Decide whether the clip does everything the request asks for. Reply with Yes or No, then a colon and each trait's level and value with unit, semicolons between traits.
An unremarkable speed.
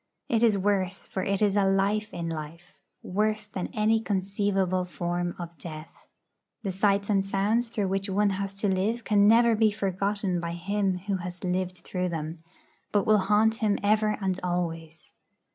Yes: average, 175 wpm